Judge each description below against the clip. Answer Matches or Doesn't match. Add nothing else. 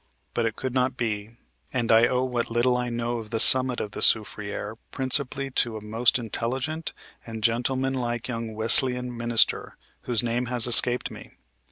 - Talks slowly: Doesn't match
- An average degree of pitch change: Doesn't match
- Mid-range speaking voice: Doesn't match